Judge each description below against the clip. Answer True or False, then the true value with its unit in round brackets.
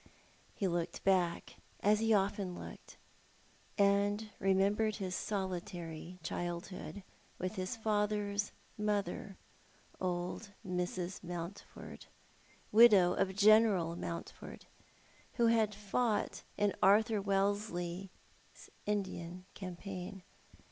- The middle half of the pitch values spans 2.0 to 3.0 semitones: True (2.5 semitones)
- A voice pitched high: True (195 Hz)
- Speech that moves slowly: True (95 wpm)